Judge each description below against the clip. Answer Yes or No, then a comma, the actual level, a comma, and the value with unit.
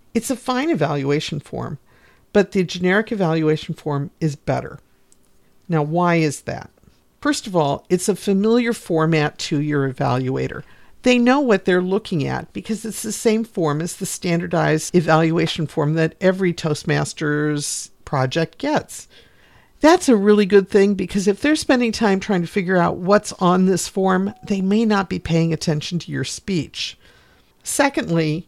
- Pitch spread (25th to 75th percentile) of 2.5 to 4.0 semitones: No, average, 5.1 semitones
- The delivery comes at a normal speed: Yes, average, 160 wpm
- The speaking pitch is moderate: Yes, medium, 180 Hz